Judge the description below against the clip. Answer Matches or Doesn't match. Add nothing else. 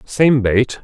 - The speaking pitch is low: Matches